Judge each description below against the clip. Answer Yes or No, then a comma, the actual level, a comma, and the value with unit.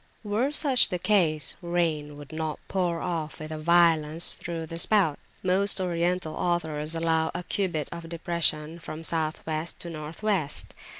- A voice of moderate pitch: Yes, medium, 165 Hz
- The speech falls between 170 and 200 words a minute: No, average, 155 wpm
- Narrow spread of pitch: Yes, narrow, 2.3 semitones